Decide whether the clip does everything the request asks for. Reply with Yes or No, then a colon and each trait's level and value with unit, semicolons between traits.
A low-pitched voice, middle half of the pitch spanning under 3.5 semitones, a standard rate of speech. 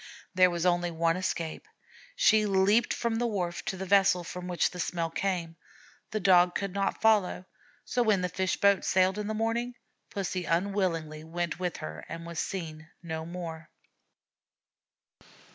No: medium, 180 Hz; average, 2.9 semitones; average, 160 wpm